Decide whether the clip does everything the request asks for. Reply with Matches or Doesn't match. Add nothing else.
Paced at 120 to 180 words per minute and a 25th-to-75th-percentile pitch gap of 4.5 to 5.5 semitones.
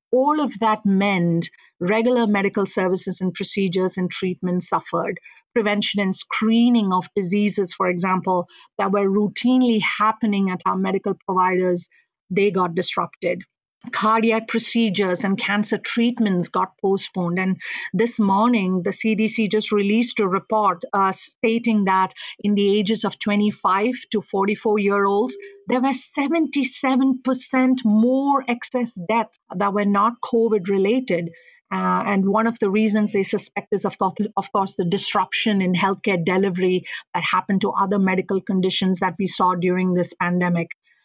Doesn't match